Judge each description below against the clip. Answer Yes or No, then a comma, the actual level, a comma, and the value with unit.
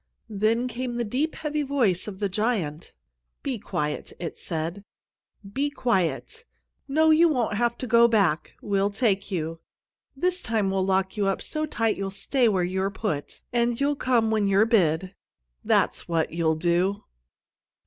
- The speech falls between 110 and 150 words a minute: No, average, 160 wpm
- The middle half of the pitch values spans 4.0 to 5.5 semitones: Yes, average, 4.6 semitones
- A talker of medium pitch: No, high, 210 Hz